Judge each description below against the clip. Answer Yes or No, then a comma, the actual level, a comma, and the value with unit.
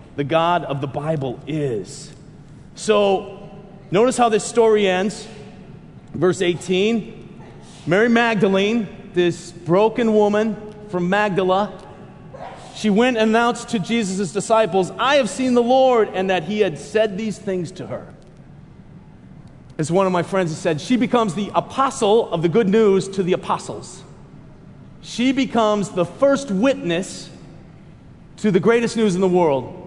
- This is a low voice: No, high, 195 Hz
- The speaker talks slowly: No, average, 145 wpm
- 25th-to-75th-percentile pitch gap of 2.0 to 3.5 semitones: No, average, 4.0 semitones